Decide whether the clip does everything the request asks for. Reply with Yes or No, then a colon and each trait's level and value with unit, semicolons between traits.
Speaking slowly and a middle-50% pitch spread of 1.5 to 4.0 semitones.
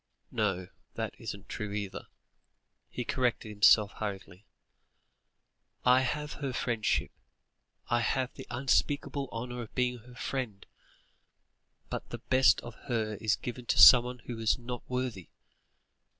Yes: slow, 130 wpm; average, 2.9 semitones